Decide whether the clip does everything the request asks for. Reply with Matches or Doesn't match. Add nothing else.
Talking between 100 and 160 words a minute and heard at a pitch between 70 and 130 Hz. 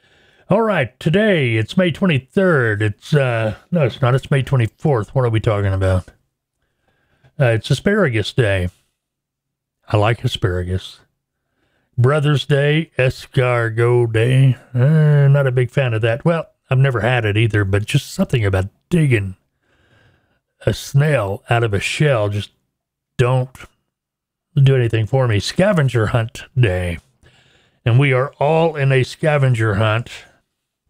Matches